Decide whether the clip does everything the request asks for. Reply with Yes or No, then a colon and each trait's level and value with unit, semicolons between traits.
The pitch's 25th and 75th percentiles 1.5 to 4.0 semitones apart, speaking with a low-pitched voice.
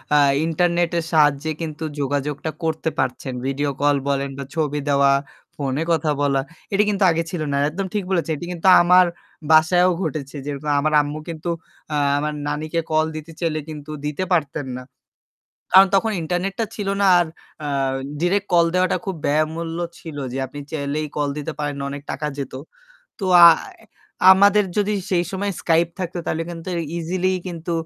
No: average, 3.3 semitones; medium, 160 Hz